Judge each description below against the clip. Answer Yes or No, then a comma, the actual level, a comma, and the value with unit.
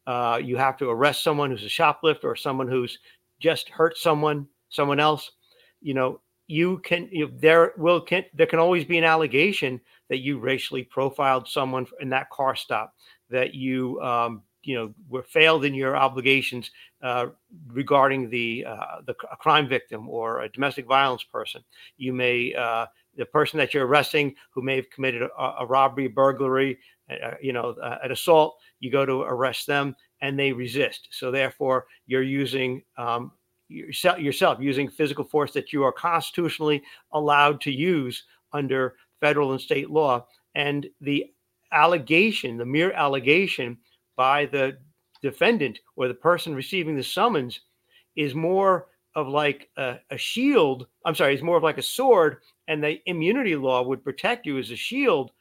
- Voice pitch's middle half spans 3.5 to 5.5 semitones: No, average, 3.0 semitones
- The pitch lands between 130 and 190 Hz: Yes, medium, 140 Hz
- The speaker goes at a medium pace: Yes, average, 165 wpm